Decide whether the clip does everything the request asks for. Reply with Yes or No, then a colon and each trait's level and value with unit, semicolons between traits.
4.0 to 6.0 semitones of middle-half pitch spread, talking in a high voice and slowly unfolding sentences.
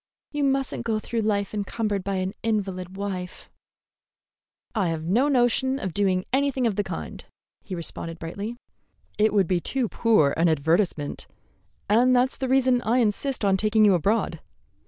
No: average, 4.7 semitones; high, 210 Hz; average, 160 wpm